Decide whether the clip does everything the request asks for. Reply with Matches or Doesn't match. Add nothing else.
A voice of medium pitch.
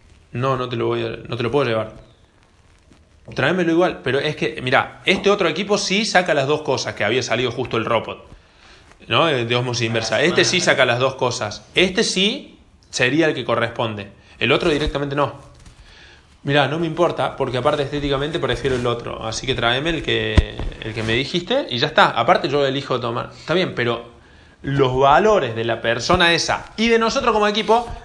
Doesn't match